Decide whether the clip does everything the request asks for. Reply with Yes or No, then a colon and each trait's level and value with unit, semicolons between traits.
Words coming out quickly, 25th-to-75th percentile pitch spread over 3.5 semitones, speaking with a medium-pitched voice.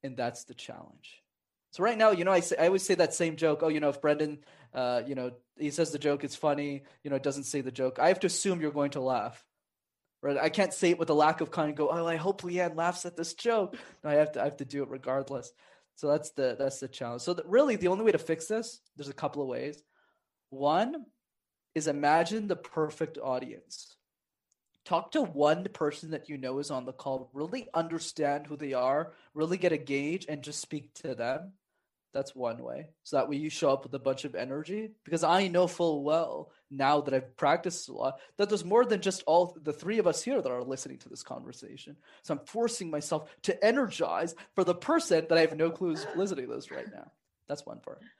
Yes: fast, 240 wpm; average, 4.1 semitones; medium, 155 Hz